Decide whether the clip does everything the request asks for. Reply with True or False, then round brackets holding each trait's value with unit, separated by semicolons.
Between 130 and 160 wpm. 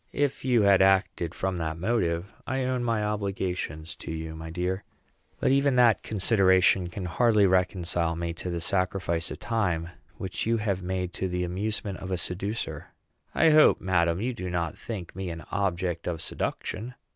False (175 wpm)